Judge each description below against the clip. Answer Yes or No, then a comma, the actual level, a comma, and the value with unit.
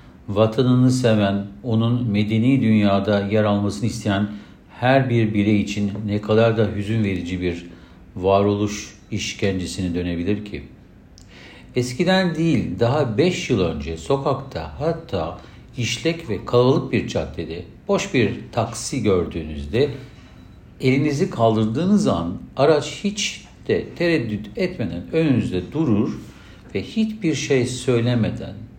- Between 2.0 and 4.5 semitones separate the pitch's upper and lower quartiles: No, average, 5.1 semitones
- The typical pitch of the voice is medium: No, low, 110 Hz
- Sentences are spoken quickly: No, average, 110 wpm